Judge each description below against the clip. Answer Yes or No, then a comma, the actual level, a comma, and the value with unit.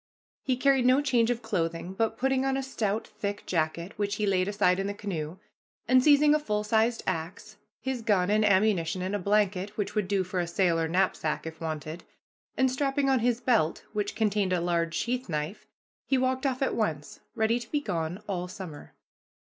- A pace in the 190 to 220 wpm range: Yes, average, 200 wpm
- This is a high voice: Yes, high, 205 Hz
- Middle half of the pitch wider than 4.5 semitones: Yes, average, 5.3 semitones